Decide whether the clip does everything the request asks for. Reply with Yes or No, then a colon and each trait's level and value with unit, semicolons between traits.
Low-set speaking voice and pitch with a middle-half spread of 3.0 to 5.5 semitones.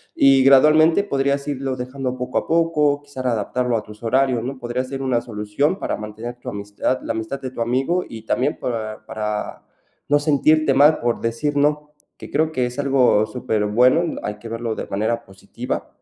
Yes: low, 130 Hz; average, 3.8 semitones